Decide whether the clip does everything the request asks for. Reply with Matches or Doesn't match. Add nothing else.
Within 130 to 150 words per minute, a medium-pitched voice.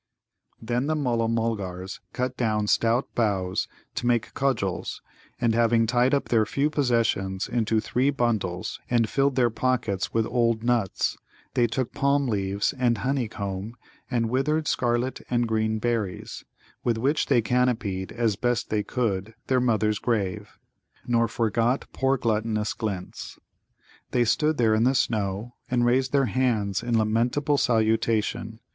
Doesn't match